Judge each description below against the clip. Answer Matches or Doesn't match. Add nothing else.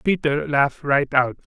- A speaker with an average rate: Matches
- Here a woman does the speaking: Doesn't match